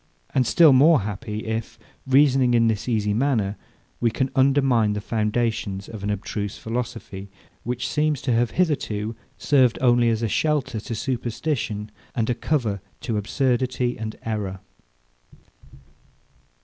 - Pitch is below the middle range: Yes, low, 115 Hz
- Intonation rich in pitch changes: No, average, 3.4 semitones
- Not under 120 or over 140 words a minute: Yes, slow, 135 wpm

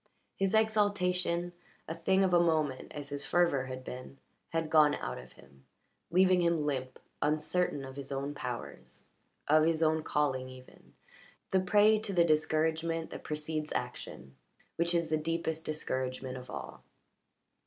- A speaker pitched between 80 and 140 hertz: No, medium, 155 Hz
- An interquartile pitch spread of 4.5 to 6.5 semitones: No, average, 3.8 semitones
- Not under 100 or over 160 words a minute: Yes, average, 155 wpm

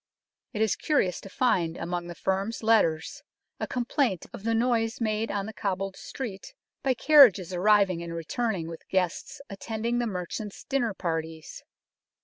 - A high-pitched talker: Yes, high, 205 Hz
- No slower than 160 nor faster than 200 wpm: No, average, 150 wpm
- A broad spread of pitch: No, average, 4.5 semitones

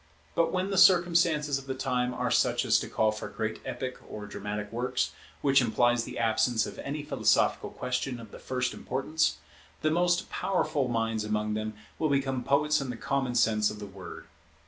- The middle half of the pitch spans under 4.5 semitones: No, average, 4.9 semitones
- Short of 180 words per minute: No, average, 190 wpm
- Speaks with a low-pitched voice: Yes, low, 125 Hz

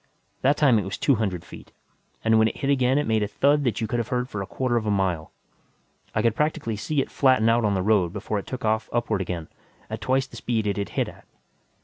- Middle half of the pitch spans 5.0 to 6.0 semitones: No, average, 4.0 semitones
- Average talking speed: No, fast, 260 wpm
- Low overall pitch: Yes, low, 110 Hz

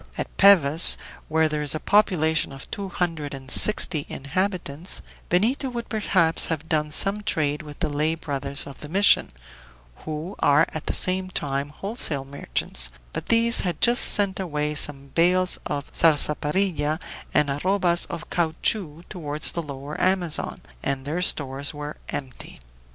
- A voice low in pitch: No, medium, 155 Hz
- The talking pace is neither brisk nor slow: Yes, average, 150 wpm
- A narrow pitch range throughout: No, average, 4.1 semitones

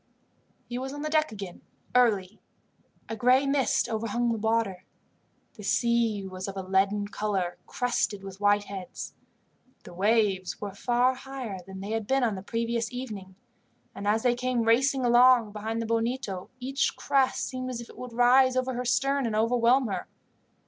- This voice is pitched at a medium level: No, high, 230 Hz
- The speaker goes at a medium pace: Yes, average, 170 wpm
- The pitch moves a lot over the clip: No, average, 3.7 semitones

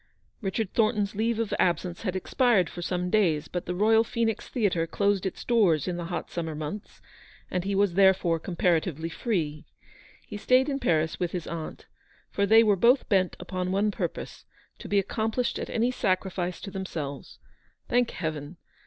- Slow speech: No, average, 175 wpm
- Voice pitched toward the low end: No, high, 190 Hz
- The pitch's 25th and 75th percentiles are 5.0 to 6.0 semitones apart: No, average, 4.0 semitones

